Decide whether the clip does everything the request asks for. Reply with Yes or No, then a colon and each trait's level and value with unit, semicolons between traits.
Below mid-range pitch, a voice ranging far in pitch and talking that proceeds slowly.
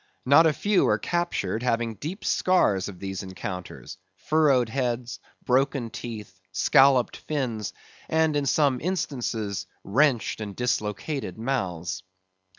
Yes: low, 120 Hz; wide, 6.3 semitones; slow, 120 wpm